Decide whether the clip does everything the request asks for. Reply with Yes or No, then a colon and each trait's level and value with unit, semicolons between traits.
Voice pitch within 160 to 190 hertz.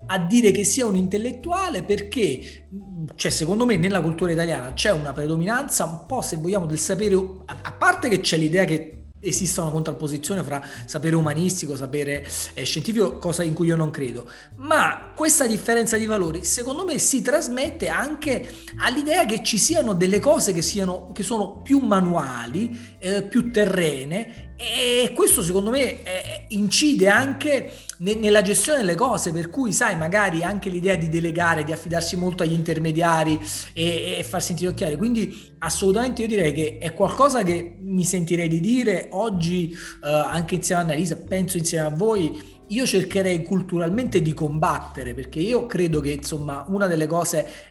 Yes: medium, 185 Hz